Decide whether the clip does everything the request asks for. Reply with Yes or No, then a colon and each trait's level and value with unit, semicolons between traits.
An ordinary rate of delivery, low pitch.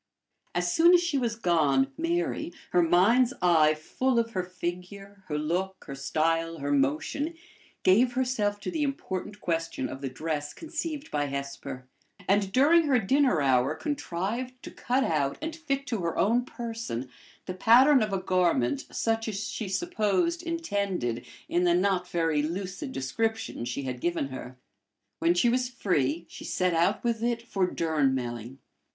No: average, 160 wpm; medium, 185 Hz